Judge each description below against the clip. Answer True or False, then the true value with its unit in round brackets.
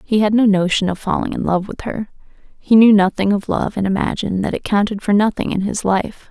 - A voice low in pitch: False (200 Hz)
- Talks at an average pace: False (240 wpm)